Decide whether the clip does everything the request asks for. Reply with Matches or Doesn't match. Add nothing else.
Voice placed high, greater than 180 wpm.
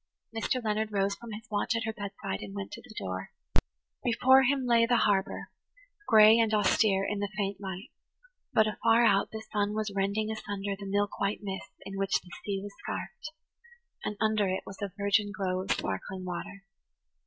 Matches